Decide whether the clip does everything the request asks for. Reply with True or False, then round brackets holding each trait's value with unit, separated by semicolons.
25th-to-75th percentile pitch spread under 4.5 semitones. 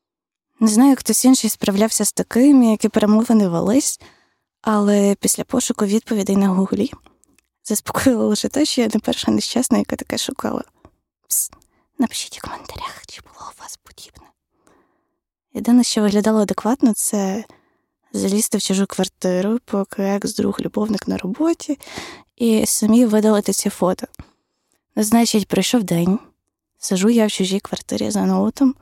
True (3.3 semitones)